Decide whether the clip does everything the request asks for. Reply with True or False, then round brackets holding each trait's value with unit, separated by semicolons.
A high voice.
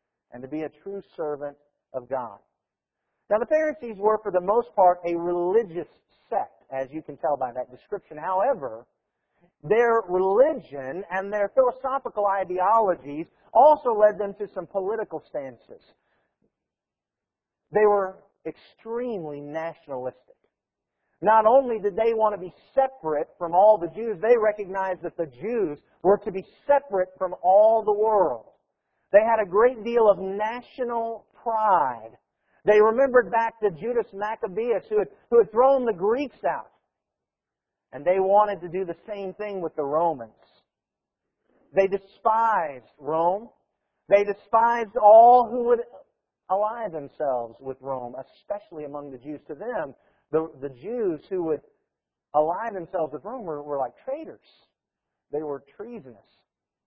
True (200 Hz)